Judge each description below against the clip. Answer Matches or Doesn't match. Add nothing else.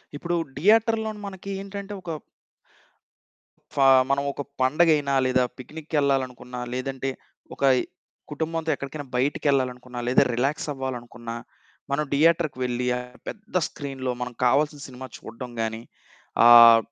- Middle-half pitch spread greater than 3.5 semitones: Matches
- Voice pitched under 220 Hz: Matches